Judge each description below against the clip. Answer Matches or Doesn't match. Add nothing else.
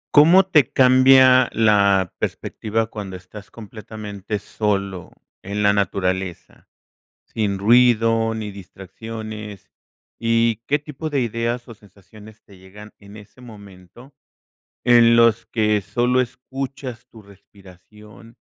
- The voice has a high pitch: Doesn't match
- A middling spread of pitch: Matches